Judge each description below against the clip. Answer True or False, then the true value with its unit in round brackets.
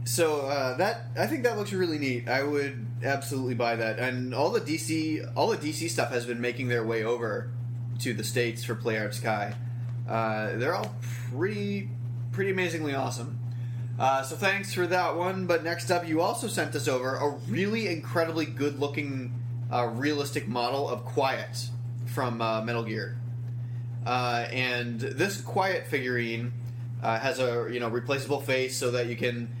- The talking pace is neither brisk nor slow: True (170 wpm)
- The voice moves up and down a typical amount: False (2.1 semitones)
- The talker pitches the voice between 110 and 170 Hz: True (120 Hz)